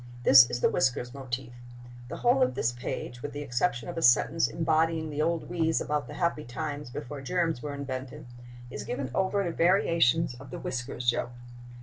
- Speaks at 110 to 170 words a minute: No, average, 190 wpm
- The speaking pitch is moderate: Yes, medium, 145 Hz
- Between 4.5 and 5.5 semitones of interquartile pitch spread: Yes, average, 4.9 semitones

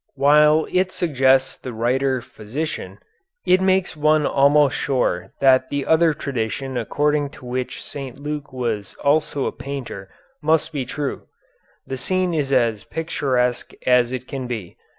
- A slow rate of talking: No, average, 145 wpm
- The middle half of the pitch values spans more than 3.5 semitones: No, average, 3.2 semitones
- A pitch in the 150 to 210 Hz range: No, low, 135 Hz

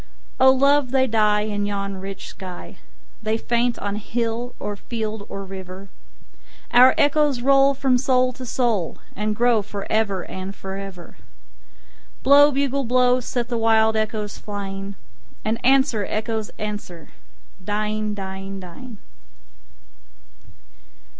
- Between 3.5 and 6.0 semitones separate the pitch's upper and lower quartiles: Yes, average, 4.0 semitones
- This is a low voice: No, high, 220 Hz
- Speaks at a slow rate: Yes, slow, 115 wpm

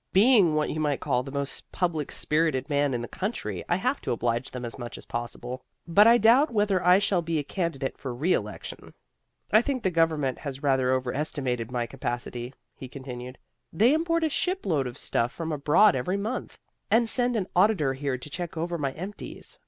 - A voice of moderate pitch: Yes, medium, 150 Hz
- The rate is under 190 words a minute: No, average, 195 wpm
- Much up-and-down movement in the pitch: Yes, wide, 7.1 semitones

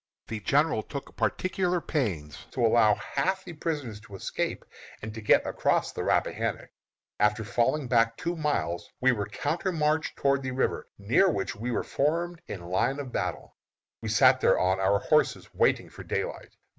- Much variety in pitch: Yes, wide, 6.8 semitones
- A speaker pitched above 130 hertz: No, low, 125 Hz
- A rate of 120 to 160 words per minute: No, average, 170 wpm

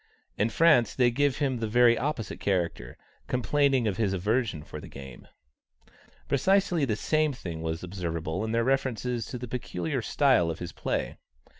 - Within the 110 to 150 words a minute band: No, average, 165 wpm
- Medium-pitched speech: No, low, 115 Hz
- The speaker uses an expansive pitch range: Yes, wide, 6.7 semitones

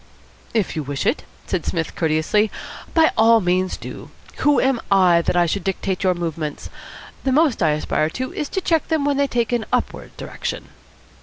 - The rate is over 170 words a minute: Yes, average, 185 wpm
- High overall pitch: Yes, high, 195 Hz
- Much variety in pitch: Yes, wide, 7.7 semitones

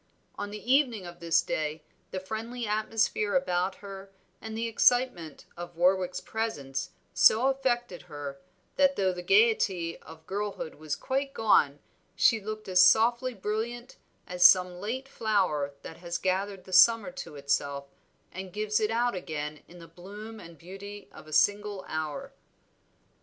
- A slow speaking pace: No, average, 150 wpm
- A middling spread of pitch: Yes, average, 4.5 semitones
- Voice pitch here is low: No, high, 195 Hz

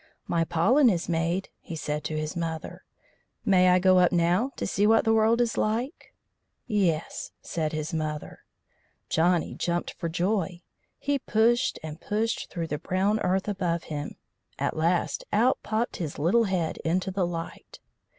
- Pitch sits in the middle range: Yes, medium, 180 Hz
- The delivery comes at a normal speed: Yes, average, 160 wpm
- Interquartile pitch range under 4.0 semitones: No, average, 4.5 semitones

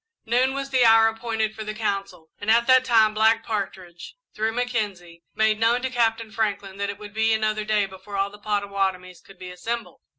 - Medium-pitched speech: No, high, 215 Hz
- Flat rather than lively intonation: Yes, narrow, 2.3 semitones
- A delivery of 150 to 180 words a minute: No, average, 200 wpm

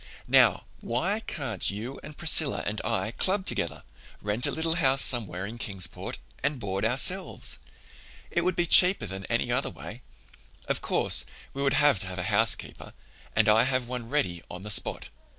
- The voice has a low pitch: Yes, low, 120 Hz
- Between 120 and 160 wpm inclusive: No, average, 175 wpm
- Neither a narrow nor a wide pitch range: No, wide, 6.3 semitones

